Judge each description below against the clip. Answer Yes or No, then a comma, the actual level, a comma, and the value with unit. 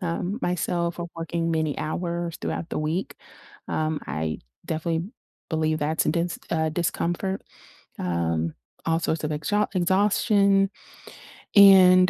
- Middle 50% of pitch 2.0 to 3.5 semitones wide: Yes, average, 2.7 semitones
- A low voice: No, medium, 170 Hz